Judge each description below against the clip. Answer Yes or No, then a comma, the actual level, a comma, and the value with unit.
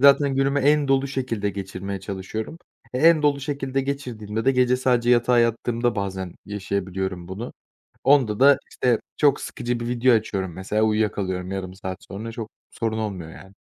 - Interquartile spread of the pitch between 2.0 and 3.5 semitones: No, average, 5.2 semitones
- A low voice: Yes, low, 115 Hz